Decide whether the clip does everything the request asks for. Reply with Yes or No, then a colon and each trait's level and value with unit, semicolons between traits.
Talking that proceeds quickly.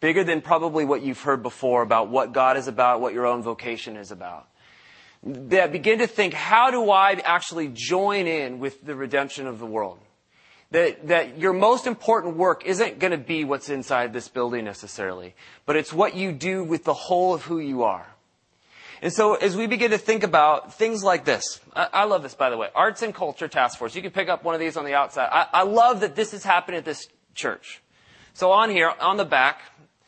Yes: fast, 220 wpm